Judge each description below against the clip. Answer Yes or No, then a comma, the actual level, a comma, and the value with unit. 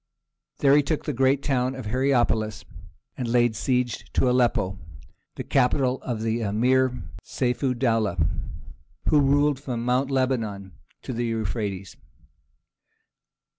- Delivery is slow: Yes, slow, 130 wpm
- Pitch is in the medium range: No, low, 125 Hz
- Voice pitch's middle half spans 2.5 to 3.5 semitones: Yes, average, 2.9 semitones